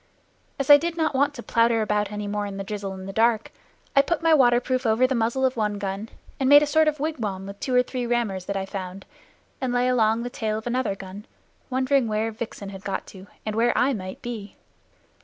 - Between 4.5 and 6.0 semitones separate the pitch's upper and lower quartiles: No, average, 4.1 semitones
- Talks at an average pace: No, fast, 230 wpm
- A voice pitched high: Yes, high, 225 Hz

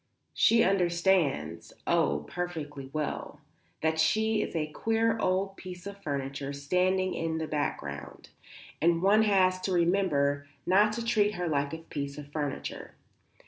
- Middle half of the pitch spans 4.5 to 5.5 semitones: Yes, average, 4.9 semitones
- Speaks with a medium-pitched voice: Yes, medium, 175 Hz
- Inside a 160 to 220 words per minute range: No, average, 140 wpm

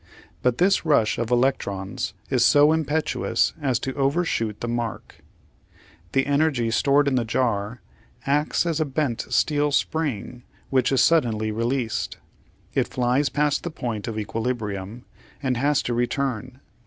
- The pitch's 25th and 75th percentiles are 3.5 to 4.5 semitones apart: Yes, average, 4.0 semitones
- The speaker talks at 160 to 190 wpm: No, average, 140 wpm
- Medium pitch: No, low, 130 Hz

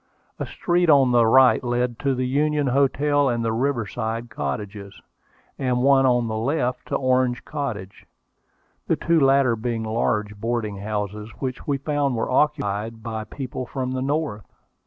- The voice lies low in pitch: Yes, low, 125 Hz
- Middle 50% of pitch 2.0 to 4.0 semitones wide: Yes, average, 3.7 semitones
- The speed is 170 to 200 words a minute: No, average, 155 wpm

